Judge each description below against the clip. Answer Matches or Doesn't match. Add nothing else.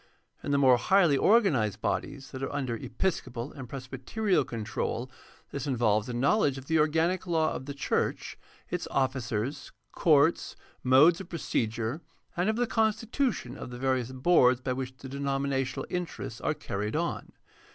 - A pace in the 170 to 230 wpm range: Doesn't match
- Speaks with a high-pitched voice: Doesn't match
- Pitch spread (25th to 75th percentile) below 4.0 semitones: Doesn't match